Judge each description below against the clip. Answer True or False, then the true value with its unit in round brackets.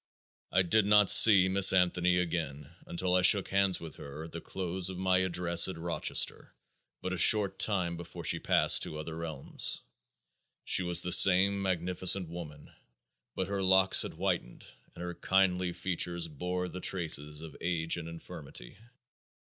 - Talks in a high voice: False (90 Hz)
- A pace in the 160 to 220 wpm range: True (165 wpm)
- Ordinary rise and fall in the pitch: False (2.1 semitones)